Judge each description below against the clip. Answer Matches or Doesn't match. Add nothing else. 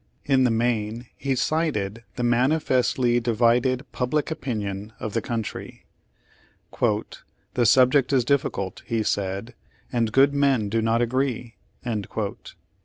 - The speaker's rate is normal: Doesn't match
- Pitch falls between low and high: Doesn't match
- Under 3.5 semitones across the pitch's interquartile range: Matches